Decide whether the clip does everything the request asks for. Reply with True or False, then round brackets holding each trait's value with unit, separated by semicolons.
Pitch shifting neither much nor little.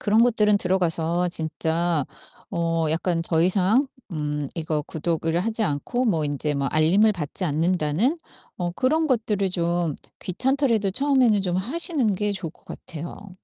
True (4.9 semitones)